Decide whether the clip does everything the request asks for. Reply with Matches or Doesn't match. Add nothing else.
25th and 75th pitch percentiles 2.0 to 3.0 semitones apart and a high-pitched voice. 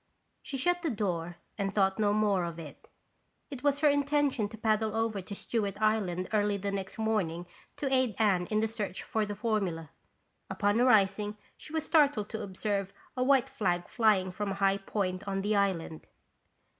Matches